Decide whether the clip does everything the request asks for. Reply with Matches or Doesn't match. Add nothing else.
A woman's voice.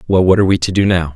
Doesn't match